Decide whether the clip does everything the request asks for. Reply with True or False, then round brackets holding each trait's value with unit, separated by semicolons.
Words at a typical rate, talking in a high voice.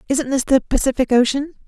True (180 wpm; 265 Hz)